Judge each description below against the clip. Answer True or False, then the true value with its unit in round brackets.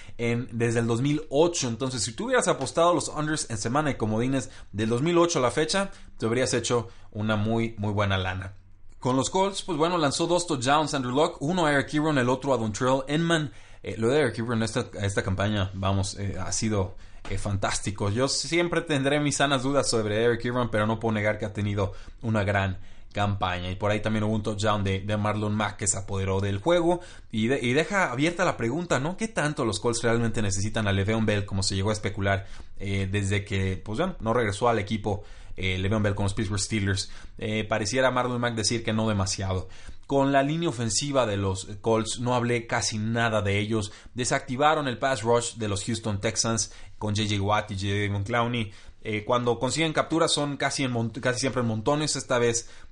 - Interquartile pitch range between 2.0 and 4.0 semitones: False (4.7 semitones)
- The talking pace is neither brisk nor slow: False (205 wpm)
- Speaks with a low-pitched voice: True (115 Hz)